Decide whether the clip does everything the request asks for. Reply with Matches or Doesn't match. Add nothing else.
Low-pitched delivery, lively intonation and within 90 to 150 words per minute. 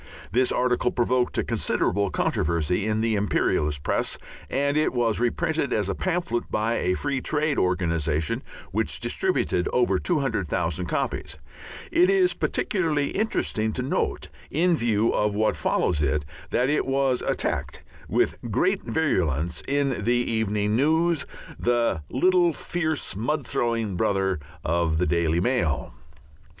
Matches